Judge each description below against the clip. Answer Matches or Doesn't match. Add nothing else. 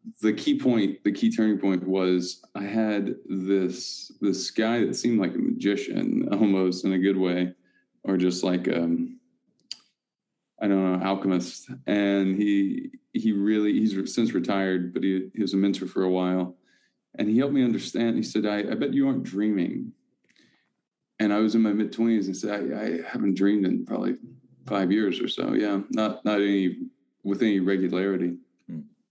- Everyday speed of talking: Matches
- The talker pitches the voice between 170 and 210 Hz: Doesn't match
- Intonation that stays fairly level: Doesn't match